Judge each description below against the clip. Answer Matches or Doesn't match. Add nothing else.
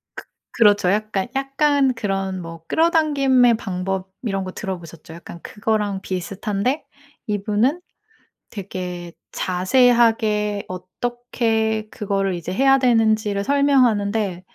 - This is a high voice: Matches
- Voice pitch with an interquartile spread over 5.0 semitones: Doesn't match